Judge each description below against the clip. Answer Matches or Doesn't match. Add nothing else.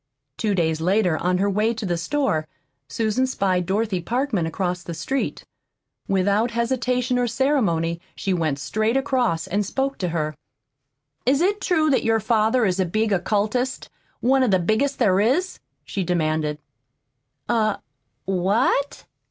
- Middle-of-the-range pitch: Doesn't match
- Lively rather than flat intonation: Matches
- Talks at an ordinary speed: Matches